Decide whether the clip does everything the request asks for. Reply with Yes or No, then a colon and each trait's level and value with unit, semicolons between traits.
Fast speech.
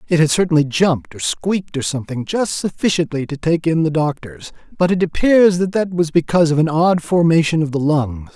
Yes: fast, 210 wpm